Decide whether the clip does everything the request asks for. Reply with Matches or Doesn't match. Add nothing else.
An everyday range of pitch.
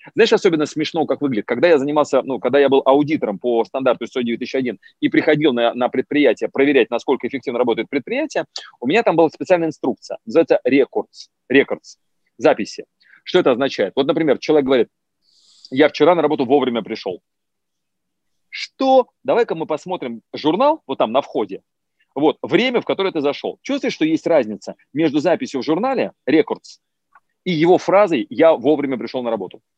Doesn't match